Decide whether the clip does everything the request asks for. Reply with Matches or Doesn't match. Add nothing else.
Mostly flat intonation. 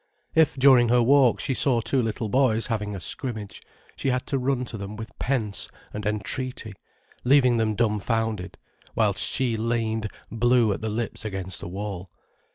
Doesn't match